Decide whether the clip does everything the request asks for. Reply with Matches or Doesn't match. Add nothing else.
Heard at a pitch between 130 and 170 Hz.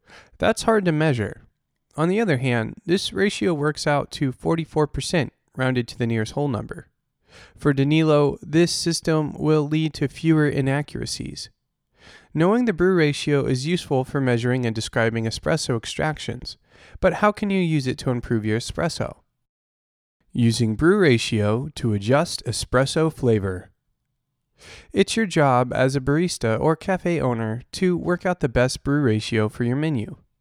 Matches